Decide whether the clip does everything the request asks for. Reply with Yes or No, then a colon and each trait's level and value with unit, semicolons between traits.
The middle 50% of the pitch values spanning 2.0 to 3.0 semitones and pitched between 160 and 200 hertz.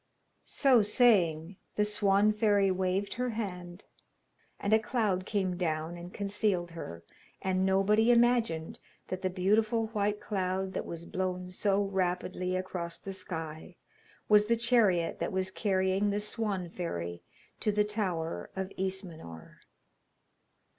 Yes: average, 2.7 semitones; high, 190 Hz